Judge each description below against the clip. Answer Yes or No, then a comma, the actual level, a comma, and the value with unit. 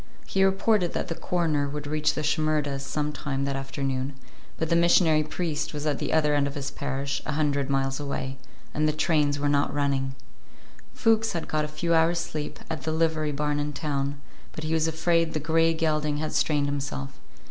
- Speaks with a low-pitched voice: No, medium, 150 Hz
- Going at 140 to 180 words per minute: No, average, 195 wpm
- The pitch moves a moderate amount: No, narrow, 2.2 semitones